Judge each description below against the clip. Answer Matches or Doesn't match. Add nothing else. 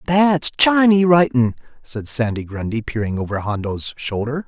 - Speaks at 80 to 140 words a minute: Matches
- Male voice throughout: Matches